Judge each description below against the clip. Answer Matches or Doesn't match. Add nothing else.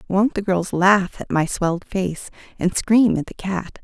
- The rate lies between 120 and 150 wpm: Doesn't match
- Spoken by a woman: Matches